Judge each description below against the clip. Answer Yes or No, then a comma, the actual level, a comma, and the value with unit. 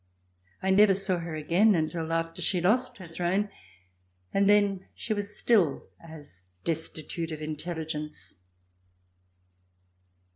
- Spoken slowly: Yes, slow, 115 wpm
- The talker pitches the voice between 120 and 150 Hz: No, medium, 170 Hz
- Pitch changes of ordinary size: Yes, average, 3.8 semitones